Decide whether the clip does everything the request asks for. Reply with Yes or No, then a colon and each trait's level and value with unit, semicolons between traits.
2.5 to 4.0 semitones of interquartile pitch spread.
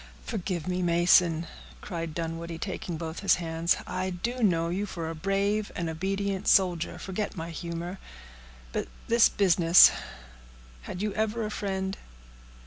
Yes: average, 3.0 semitones